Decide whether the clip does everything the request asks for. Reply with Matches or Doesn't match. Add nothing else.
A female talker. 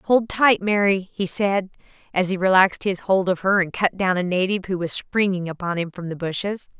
Matches